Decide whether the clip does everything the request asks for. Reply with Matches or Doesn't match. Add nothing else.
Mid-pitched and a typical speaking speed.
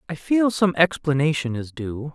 Matches